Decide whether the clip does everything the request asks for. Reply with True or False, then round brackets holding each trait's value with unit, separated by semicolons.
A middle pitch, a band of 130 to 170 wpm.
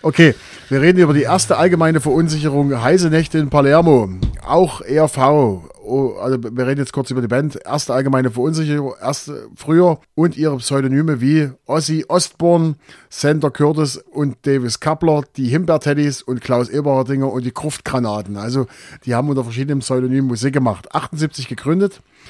True (145 Hz; 150 wpm)